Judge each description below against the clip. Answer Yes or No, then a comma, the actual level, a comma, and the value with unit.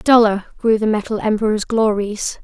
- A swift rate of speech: No, average, 150 wpm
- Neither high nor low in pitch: No, high, 215 Hz